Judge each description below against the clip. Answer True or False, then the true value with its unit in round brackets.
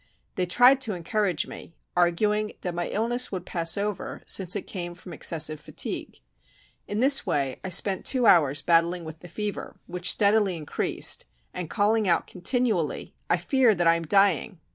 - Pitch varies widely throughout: False (3.8 semitones)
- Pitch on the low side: False (185 Hz)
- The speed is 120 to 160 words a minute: False (170 wpm)